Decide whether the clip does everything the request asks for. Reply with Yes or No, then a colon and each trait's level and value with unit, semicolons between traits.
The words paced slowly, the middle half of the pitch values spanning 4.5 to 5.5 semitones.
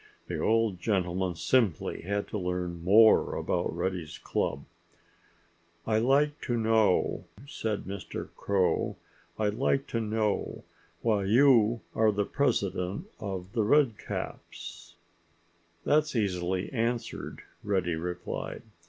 No: slow, 110 wpm; average, 3.9 semitones